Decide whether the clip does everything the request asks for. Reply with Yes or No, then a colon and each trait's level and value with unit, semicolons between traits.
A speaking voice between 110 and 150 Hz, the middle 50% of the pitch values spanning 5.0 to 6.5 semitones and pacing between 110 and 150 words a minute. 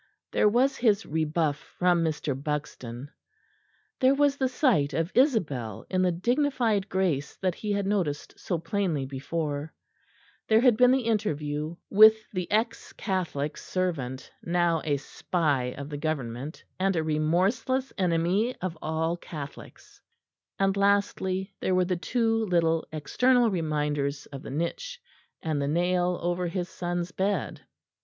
No: medium, 175 Hz; average, 5.3 semitones; average, 140 wpm